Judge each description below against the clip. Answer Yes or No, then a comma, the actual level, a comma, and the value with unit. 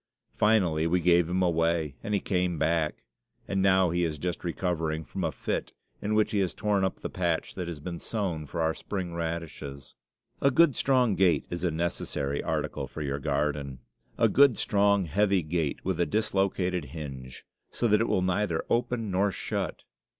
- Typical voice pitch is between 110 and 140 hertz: No, very low, 90 Hz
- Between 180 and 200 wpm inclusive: Yes, average, 185 wpm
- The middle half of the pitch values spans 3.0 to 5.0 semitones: Yes, average, 3.7 semitones